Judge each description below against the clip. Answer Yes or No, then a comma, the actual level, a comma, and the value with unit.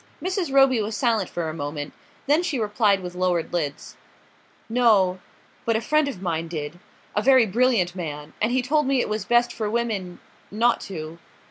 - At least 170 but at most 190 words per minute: Yes, average, 180 wpm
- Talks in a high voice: Yes, high, 210 Hz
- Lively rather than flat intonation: Yes, wide, 5.8 semitones